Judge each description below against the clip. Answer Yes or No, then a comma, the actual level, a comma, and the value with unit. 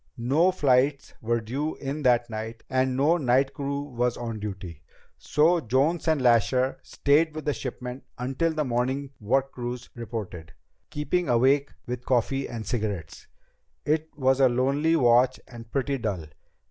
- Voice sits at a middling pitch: No, low, 130 Hz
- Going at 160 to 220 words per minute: No, average, 150 wpm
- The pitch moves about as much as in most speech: Yes, average, 3.2 semitones